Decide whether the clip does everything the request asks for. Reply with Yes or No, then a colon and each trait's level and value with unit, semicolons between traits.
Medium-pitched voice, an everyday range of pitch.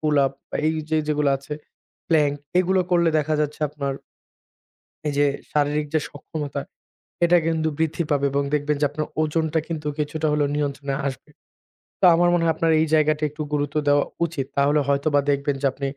No: medium, 150 Hz; narrow, 1.7 semitones